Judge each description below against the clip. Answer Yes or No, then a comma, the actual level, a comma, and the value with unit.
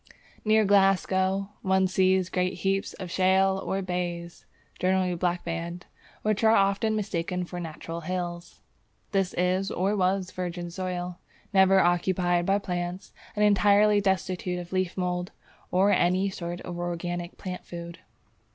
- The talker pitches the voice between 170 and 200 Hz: Yes, medium, 185 Hz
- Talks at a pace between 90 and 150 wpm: Yes, slow, 135 wpm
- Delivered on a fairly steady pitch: Yes, narrow, 1.6 semitones